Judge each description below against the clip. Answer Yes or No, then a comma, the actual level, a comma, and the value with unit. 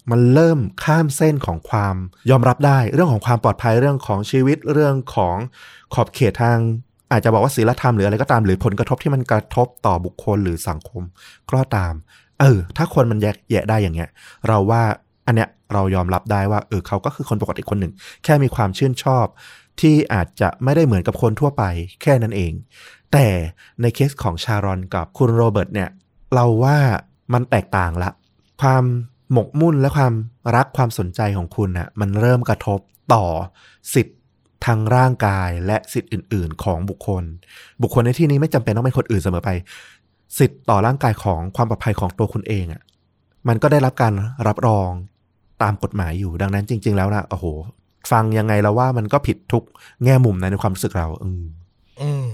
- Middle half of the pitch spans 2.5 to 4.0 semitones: No, average, 4.4 semitones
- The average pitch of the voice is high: No, low, 110 Hz